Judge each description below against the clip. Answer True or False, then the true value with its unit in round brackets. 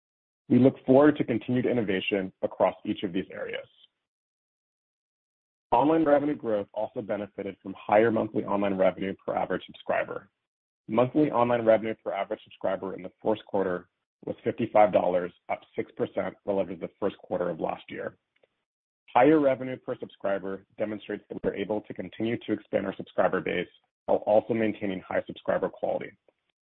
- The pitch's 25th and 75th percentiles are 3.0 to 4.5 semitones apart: True (4.1 semitones)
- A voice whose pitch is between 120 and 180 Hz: False (110 Hz)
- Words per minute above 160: False (150 wpm)